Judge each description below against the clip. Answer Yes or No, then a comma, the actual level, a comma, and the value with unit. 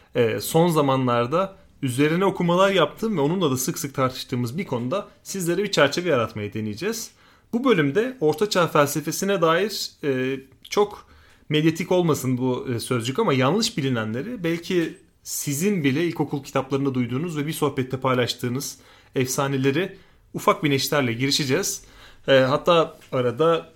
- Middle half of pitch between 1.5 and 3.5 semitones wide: No, average, 5.2 semitones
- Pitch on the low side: No, medium, 145 Hz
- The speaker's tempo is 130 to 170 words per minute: No, average, 120 wpm